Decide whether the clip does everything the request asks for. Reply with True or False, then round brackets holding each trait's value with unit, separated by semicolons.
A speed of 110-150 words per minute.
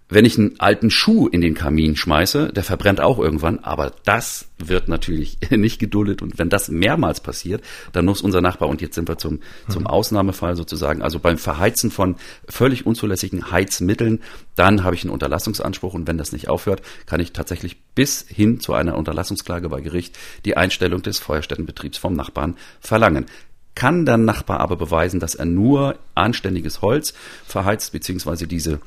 False (175 wpm)